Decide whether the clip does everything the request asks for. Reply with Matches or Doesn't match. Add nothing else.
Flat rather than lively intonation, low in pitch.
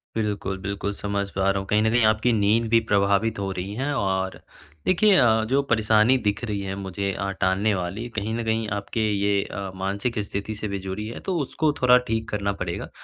Matches